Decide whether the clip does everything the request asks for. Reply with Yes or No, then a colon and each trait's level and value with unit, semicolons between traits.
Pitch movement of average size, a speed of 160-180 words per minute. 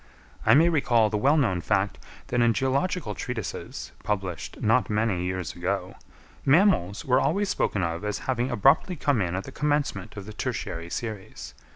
No: wide, 6.1 semitones; average, 170 wpm